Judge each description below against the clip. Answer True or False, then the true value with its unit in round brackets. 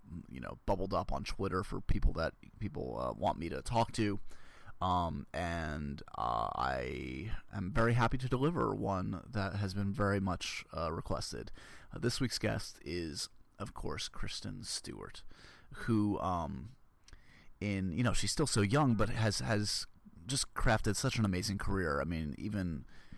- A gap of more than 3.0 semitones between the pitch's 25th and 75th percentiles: True (4.3 semitones)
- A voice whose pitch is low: True (100 Hz)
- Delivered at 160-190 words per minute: True (165 wpm)